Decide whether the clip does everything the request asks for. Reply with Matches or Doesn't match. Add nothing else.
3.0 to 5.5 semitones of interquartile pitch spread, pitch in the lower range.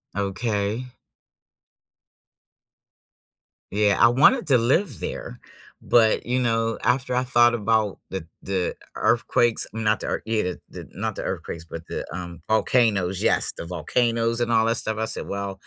Matches